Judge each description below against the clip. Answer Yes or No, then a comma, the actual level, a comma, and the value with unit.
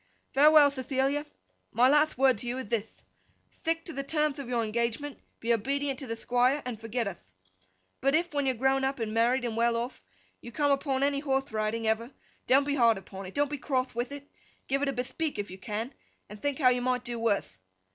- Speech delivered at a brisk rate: Yes, fast, 215 wpm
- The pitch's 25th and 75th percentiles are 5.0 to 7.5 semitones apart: No, average, 3.6 semitones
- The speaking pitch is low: No, very high, 255 Hz